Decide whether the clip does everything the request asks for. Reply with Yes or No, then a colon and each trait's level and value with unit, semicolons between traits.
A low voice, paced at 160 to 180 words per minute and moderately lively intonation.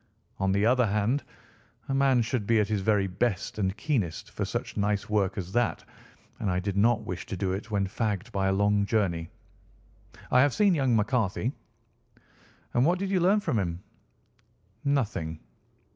Yes: low, 105 Hz; average, 175 wpm; average, 4.3 semitones